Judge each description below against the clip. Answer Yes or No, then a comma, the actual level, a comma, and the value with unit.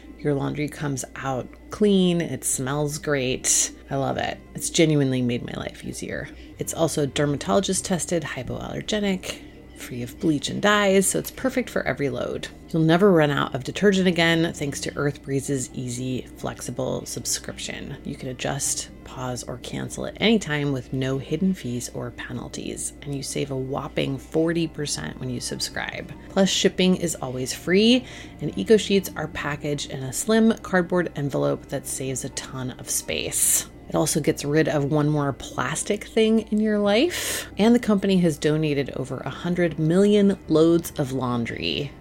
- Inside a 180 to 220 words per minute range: No, average, 165 wpm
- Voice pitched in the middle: Yes, medium, 150 Hz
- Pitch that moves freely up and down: Yes, wide, 5.7 semitones